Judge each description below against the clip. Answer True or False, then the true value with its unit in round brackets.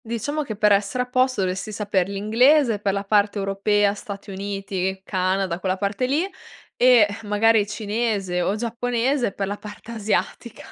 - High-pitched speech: True (205 Hz)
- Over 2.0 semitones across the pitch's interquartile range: True (2.9 semitones)